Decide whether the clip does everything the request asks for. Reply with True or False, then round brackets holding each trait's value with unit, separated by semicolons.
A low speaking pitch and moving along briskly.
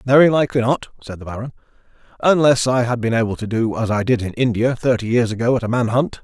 True (120 Hz; 240 wpm)